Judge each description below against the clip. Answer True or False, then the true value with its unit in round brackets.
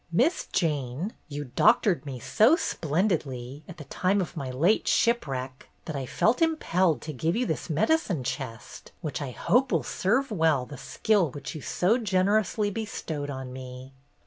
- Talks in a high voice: False (160 Hz)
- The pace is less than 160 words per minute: False (165 wpm)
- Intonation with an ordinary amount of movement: False (7.6 semitones)